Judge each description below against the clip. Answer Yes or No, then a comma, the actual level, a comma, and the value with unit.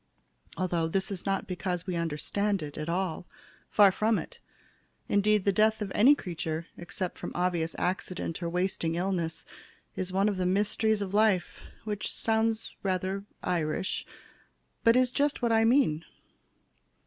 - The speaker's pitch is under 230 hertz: Yes, high, 190 Hz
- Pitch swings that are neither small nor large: Yes, average, 3.4 semitones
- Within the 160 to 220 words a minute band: No, average, 150 wpm